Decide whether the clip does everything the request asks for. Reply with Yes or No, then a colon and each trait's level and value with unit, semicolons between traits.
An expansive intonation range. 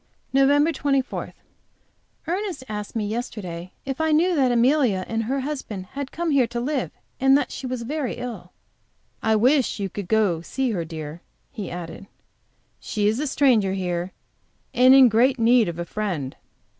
Yes: wide, 5.7 semitones